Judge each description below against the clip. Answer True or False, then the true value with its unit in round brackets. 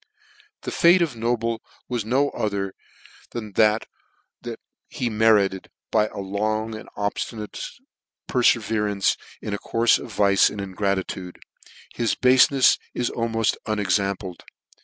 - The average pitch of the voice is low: True (110 Hz)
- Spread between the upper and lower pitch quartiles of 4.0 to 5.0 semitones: False (2.6 semitones)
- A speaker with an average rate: False (120 wpm)